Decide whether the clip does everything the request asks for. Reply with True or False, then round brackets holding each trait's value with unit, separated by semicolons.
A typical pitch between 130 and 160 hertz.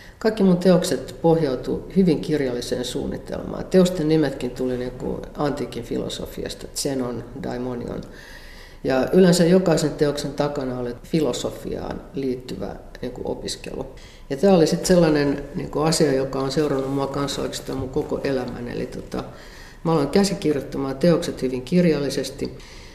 True (140 Hz)